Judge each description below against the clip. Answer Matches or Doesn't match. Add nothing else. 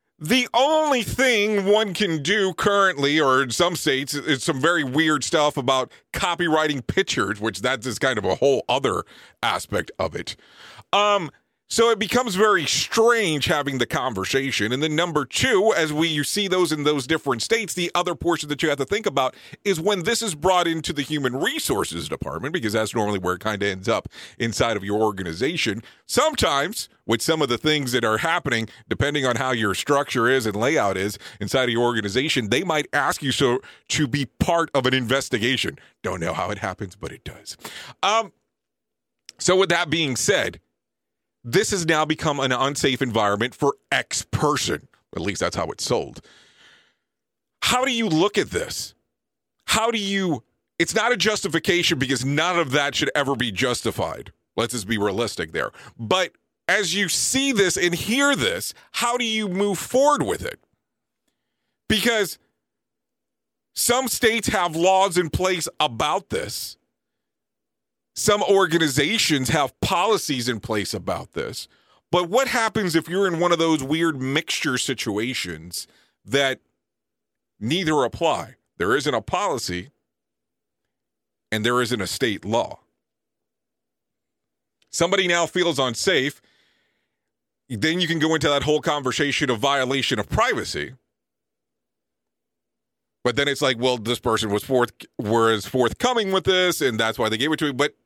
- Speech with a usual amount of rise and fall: Doesn't match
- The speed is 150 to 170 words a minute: Matches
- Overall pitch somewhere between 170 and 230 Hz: Doesn't match